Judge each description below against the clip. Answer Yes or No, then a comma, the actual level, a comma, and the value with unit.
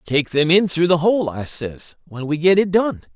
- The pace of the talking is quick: Yes, fast, 250 wpm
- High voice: No, medium, 165 Hz